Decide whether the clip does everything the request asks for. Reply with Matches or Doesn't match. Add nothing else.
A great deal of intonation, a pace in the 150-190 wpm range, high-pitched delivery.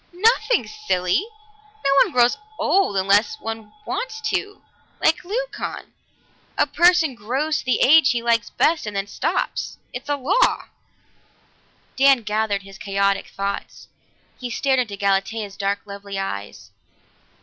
Doesn't match